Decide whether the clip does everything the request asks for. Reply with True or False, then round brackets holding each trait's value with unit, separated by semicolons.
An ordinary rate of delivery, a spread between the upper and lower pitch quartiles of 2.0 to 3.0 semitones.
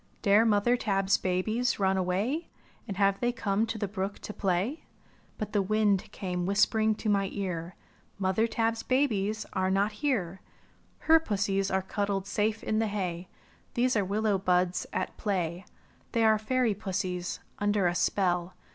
True (165 wpm; 2.6 semitones)